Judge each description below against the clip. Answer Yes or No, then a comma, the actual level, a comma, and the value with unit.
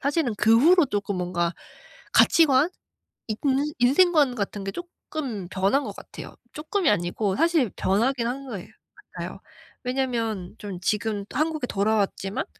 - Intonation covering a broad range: Yes, wide, 6.2 semitones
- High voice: Yes, high, 230 Hz